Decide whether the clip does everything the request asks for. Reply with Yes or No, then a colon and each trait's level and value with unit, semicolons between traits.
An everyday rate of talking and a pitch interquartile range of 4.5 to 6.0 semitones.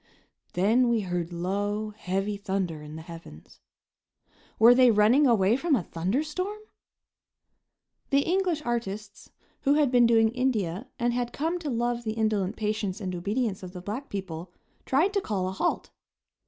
Yes: average, 160 wpm; average, 5.0 semitones